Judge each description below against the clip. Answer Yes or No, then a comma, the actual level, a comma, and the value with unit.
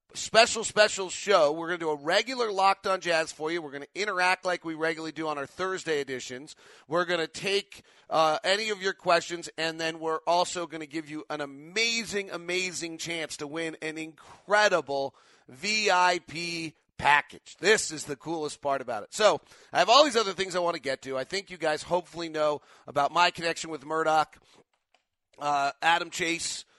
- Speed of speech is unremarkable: Yes, average, 195 wpm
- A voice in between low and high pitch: Yes, medium, 165 Hz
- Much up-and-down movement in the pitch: No, average, 3.0 semitones